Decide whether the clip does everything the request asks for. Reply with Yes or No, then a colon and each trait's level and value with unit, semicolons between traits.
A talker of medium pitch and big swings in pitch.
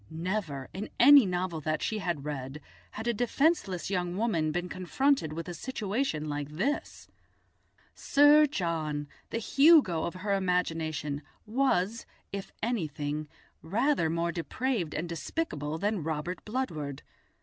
Yes: medium, 180 Hz; wide, 6.6 semitones